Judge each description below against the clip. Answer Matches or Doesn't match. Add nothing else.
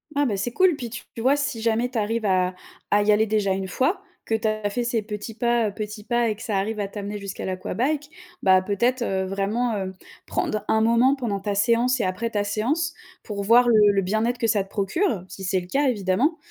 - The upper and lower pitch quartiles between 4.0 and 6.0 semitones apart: Doesn't match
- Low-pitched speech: Doesn't match